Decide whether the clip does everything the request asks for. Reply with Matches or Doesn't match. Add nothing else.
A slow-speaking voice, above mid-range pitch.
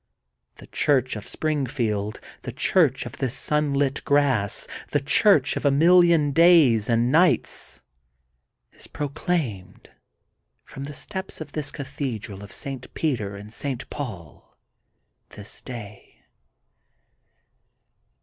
Doesn't match